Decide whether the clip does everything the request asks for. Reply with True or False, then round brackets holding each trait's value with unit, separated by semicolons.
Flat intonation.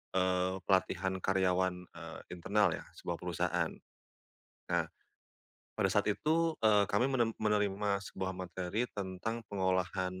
True (2.2 semitones)